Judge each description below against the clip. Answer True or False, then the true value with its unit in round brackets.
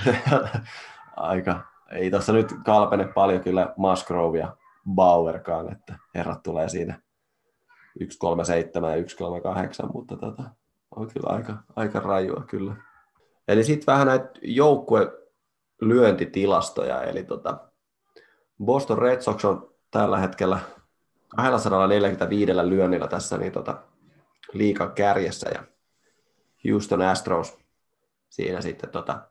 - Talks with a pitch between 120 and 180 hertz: False (100 Hz)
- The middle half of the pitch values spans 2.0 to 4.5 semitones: False (5.1 semitones)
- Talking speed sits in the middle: True (105 wpm)